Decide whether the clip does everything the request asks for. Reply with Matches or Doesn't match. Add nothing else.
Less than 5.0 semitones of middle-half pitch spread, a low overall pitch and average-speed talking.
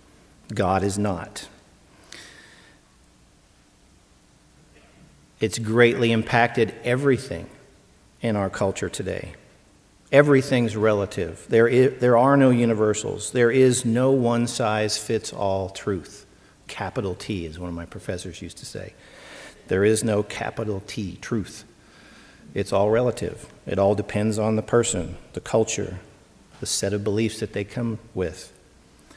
Doesn't match